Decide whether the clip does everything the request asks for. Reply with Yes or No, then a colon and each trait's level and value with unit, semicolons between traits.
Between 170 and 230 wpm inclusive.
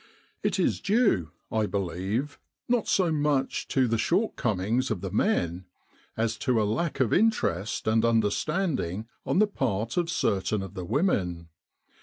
No: average, 150 wpm